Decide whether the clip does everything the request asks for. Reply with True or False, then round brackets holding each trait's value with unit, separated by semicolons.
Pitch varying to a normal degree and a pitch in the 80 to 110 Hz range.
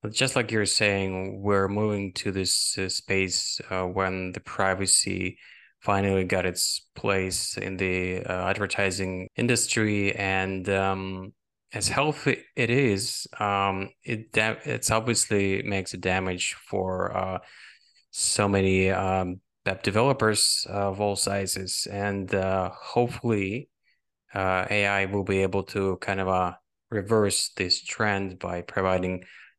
False (1.8 semitones; 95 Hz)